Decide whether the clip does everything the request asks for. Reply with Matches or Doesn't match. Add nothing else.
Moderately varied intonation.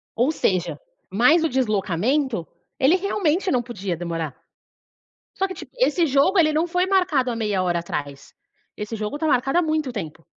Doesn't match